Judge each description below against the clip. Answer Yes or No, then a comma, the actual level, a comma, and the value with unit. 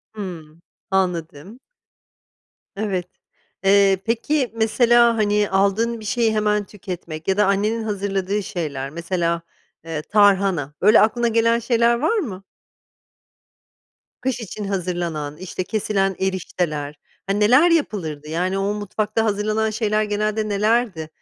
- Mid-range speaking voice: No, high, 205 Hz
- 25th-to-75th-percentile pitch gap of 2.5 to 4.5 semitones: Yes, average, 3.4 semitones